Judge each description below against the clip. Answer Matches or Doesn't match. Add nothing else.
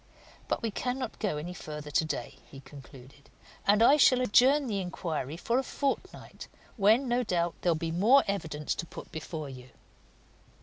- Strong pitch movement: Matches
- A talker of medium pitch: Matches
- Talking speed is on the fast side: Doesn't match